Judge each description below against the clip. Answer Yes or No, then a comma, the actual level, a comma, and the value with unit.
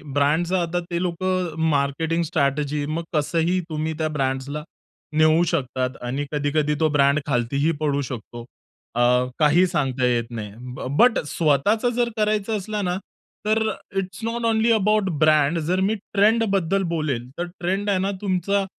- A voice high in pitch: No, medium, 160 Hz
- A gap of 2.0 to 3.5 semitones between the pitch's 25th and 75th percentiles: No, average, 5.3 semitones